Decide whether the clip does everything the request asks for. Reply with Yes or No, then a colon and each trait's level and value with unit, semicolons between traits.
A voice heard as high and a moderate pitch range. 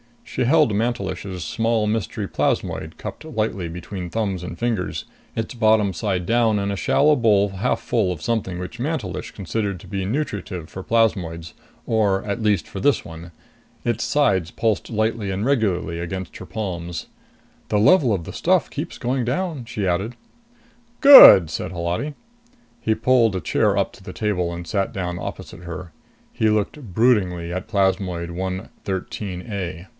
No: low, 100 Hz; average, 4.0 semitones